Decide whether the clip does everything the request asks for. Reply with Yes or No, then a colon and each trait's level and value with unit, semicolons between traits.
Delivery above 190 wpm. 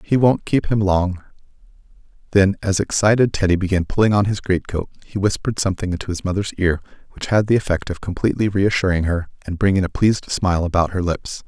Yes: average, 200 wpm